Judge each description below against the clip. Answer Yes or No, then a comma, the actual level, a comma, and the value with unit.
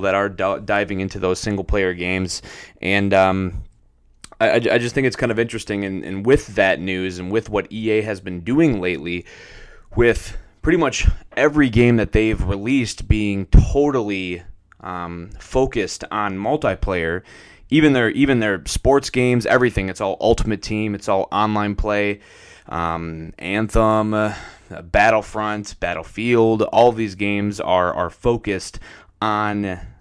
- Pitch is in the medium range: No, low, 100 Hz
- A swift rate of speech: No, average, 140 wpm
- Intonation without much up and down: No, average, 3.2 semitones